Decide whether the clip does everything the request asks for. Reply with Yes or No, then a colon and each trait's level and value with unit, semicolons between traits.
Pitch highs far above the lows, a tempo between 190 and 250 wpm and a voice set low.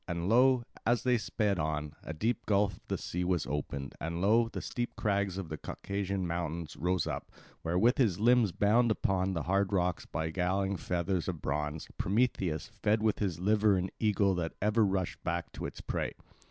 No: average, 3.7 semitones; average, 195 wpm; very low, 95 Hz